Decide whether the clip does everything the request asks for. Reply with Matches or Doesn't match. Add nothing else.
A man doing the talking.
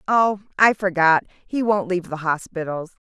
Doesn't match